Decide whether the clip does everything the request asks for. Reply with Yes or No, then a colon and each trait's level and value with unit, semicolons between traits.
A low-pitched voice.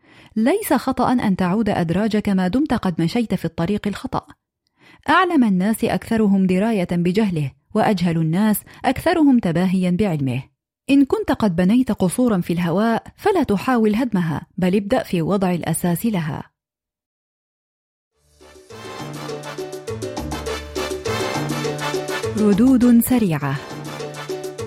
No: high, 195 Hz